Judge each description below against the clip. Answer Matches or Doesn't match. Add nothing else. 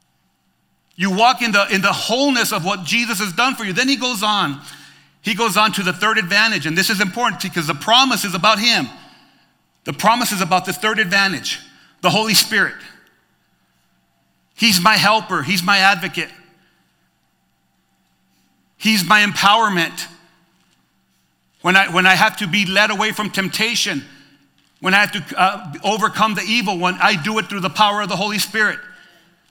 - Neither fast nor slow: Matches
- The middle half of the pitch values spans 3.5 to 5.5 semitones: Doesn't match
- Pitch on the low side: Doesn't match